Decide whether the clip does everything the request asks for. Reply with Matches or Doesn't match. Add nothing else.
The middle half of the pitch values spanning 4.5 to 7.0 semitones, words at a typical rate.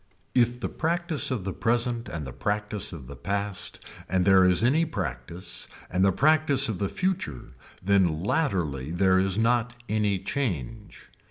Matches